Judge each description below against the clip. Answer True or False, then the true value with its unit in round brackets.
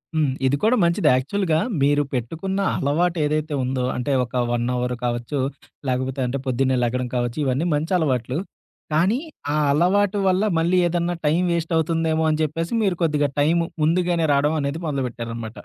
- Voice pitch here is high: False (150 Hz)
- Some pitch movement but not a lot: True (4.8 semitones)